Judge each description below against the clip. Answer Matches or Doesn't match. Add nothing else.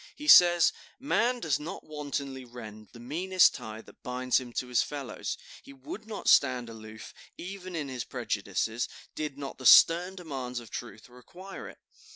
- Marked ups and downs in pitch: Matches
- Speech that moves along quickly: Doesn't match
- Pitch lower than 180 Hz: Matches